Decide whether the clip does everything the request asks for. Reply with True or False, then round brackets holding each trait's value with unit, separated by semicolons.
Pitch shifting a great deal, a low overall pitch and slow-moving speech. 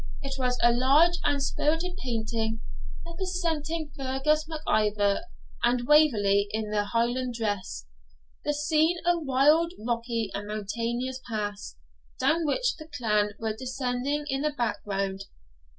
False (5.7 semitones; 250 Hz; 130 wpm)